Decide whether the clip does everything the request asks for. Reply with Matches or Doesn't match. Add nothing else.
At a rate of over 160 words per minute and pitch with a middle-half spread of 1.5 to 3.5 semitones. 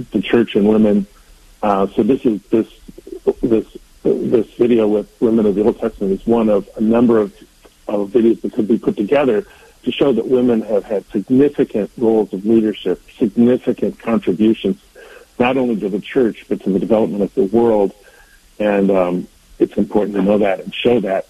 Matches